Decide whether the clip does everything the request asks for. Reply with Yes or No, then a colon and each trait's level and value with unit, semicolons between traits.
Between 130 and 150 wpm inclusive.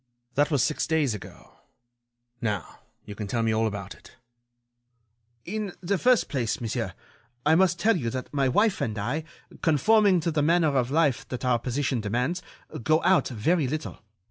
No: average, 170 wpm